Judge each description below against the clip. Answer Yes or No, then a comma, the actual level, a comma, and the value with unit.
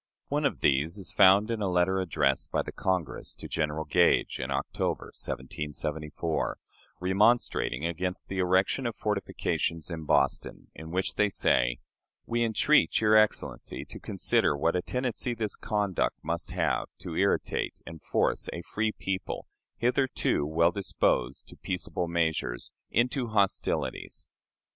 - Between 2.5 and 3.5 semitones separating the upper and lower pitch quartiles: No, average, 4.9 semitones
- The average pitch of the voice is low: Yes, very low, 90 Hz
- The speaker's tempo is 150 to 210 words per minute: No, average, 140 wpm